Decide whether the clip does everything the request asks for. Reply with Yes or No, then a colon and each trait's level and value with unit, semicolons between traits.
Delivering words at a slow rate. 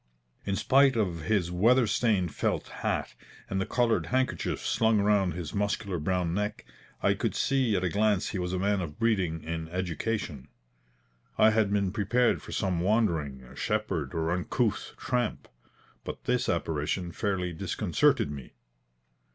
No: average, 150 wpm